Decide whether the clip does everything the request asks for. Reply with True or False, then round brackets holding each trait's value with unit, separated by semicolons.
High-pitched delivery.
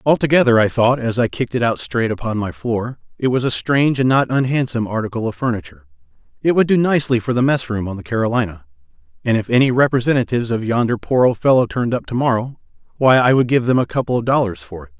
False (125 Hz)